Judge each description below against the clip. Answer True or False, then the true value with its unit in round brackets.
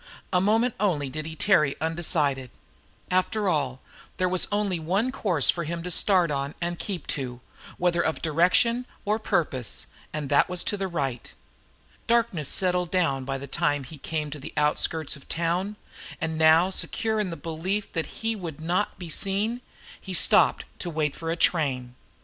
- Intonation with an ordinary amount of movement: True (4.2 semitones)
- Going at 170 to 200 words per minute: True (180 wpm)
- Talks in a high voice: False (170 Hz)